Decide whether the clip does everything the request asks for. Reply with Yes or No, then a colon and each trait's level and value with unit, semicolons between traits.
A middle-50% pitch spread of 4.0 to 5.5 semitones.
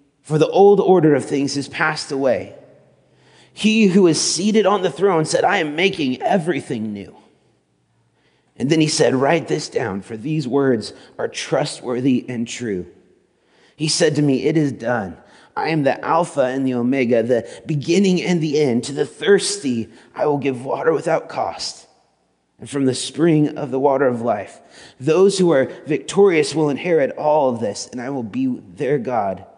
Yes: average, 4.8 semitones